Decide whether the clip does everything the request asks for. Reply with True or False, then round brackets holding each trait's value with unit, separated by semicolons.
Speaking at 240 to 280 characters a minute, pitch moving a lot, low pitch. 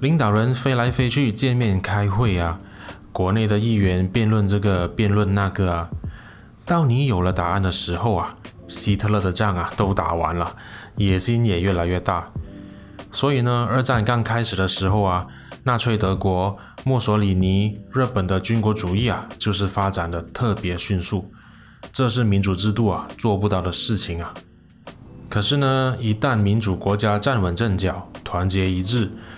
False (245 characters per minute; 3.2 semitones; 100 Hz)